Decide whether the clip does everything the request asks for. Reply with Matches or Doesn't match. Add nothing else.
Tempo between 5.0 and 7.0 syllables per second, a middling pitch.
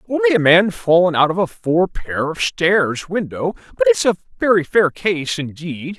Doesn't match